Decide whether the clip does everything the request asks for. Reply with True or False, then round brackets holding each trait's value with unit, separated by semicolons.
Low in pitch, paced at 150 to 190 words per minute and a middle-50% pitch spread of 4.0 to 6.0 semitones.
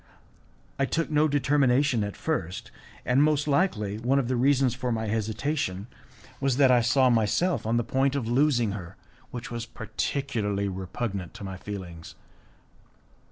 True (120 Hz; 155 wpm; 5.1 semitones)